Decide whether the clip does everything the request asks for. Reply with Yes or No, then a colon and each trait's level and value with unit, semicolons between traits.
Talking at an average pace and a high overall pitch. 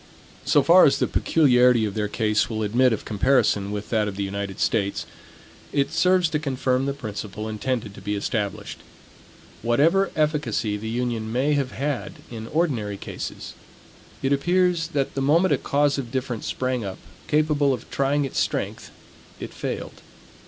No: average, 165 wpm; low, 125 Hz